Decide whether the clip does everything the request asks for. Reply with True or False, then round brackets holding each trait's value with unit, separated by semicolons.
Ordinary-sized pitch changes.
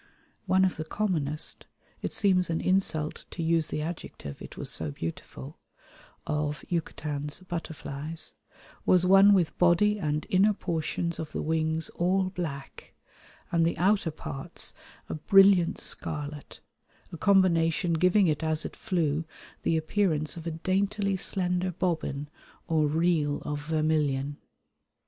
True (3.4 semitones)